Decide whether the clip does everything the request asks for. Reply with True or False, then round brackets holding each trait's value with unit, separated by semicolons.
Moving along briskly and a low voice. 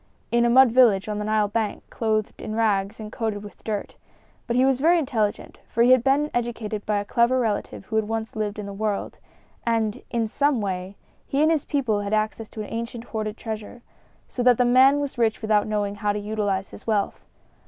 False (215 wpm; 220 Hz)